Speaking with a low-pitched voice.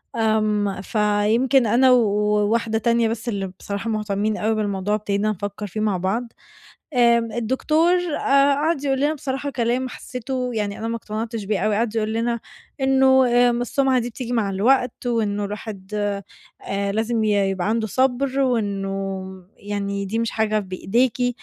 No: high, 220 Hz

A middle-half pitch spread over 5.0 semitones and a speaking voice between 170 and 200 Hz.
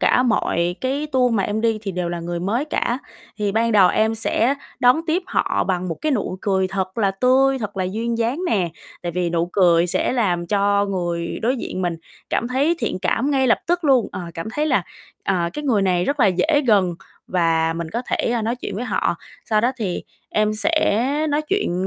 No: wide, 5.6 semitones; high, 215 Hz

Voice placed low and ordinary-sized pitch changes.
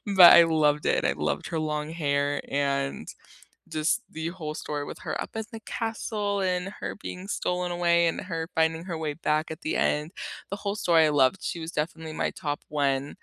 No: medium, 160 Hz; average, 3.1 semitones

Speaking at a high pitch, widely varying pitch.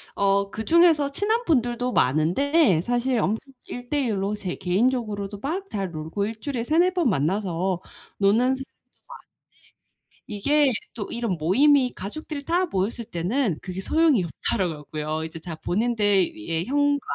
Yes: high, 220 Hz; wide, 7.1 semitones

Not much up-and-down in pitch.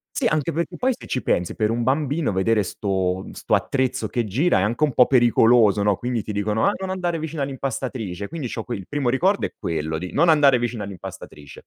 No: wide, 6.2 semitones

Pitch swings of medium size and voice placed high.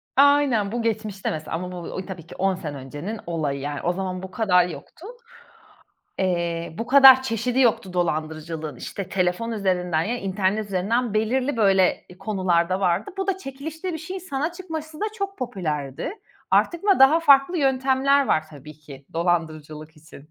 No: wide, 7.8 semitones; high, 195 Hz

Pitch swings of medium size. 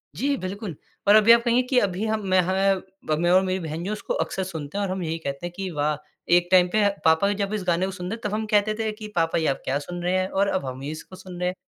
Yes: average, 3.3 semitones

